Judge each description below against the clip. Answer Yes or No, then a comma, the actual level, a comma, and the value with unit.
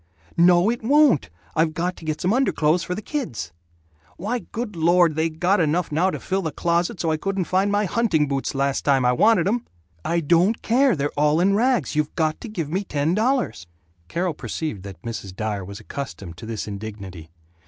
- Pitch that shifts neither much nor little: No, wide, 6.0 semitones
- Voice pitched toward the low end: No, medium, 165 Hz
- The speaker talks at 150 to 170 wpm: No, fast, 205 wpm